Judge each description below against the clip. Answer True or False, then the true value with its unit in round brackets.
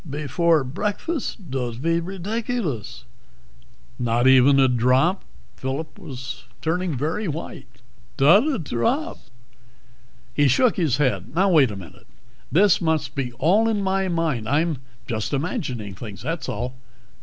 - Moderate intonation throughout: False (6.2 semitones)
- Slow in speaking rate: True (130 wpm)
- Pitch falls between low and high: True (150 Hz)